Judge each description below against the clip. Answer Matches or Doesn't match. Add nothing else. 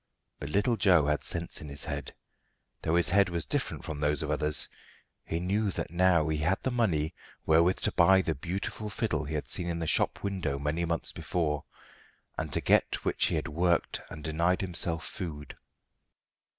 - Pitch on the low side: Matches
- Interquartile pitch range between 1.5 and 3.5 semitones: Matches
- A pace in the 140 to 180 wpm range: Doesn't match